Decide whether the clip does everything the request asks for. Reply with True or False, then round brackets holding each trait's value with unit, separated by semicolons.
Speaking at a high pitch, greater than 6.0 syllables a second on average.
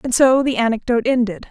True (240 Hz; 6.5 syllables/s)